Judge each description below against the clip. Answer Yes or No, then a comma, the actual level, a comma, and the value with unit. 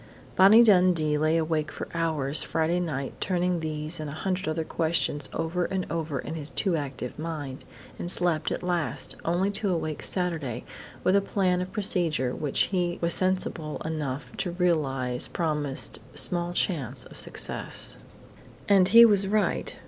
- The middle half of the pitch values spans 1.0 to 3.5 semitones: Yes, average, 3.2 semitones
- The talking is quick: No, average, 155 wpm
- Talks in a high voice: No, medium, 165 Hz